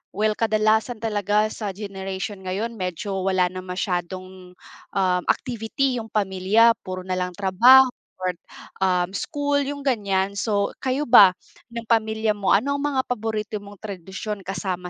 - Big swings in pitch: No, average, 3.2 semitones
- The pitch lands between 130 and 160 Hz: No, high, 205 Hz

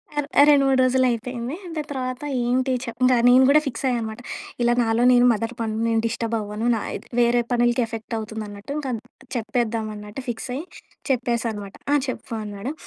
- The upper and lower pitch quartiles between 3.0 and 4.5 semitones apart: No, narrow, 2.5 semitones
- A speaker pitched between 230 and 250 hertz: Yes, high, 235 Hz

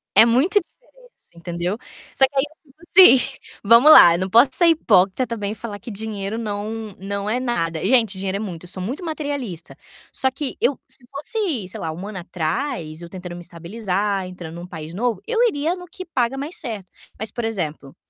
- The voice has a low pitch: No, high, 215 Hz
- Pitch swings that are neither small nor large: No, wide, 6.5 semitones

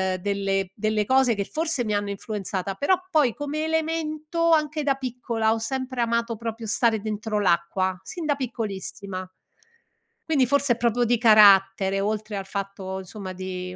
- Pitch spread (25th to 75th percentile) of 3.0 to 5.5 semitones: Yes, average, 5.0 semitones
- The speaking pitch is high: Yes, high, 220 Hz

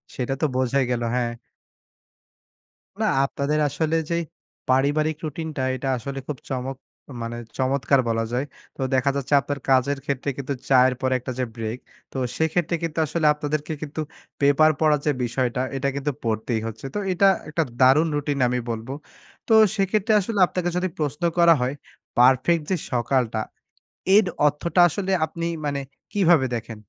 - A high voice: No, medium, 140 Hz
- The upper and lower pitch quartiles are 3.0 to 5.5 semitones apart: Yes, average, 3.6 semitones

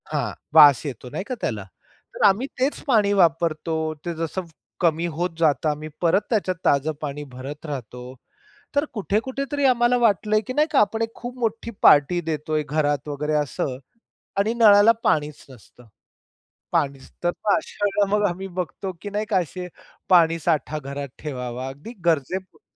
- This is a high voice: No, medium, 170 Hz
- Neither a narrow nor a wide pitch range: No, wide, 6.0 semitones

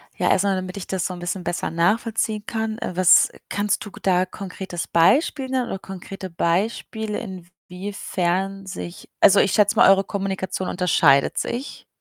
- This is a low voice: No, high, 190 Hz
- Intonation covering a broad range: No, narrow, 2.4 semitones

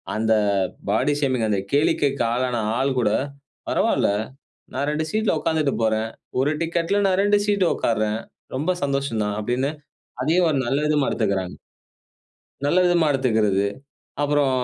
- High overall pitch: No, medium, 140 Hz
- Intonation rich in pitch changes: Yes, wide, 5.9 semitones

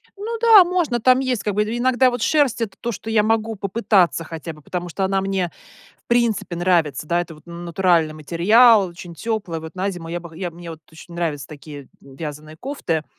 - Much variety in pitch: Yes, wide, 5.7 semitones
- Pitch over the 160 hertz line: Yes, medium, 185 Hz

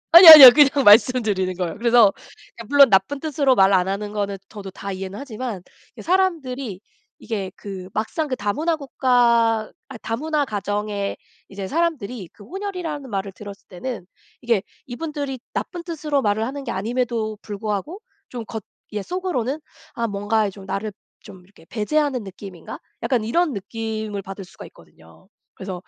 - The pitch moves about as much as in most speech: No, wide, 5.7 semitones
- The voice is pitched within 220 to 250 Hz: Yes, high, 225 Hz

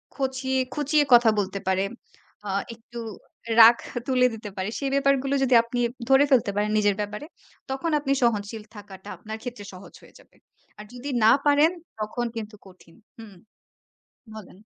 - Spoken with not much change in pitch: No, average, 4.4 semitones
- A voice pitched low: No, high, 230 Hz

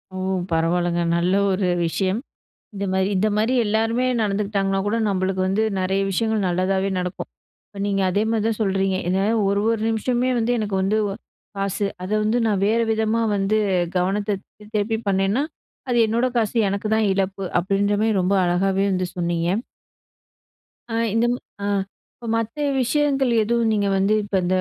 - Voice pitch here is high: Yes, high, 200 Hz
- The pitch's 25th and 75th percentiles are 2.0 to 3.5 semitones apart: Yes, narrow, 2.6 semitones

